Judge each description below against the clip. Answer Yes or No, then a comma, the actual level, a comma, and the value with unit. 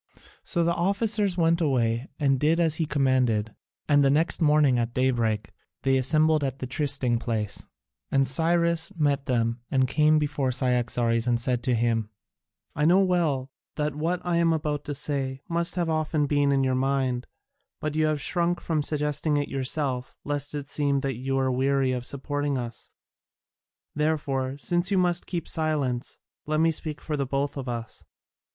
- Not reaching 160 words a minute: No, average, 175 wpm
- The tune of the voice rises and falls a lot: No, average, 3.5 semitones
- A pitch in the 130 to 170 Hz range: Yes, medium, 140 Hz